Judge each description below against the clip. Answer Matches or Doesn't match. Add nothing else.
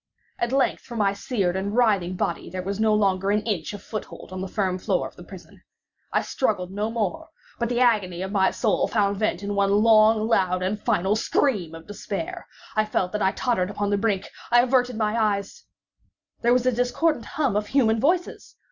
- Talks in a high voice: Matches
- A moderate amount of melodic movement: Matches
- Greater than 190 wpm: Matches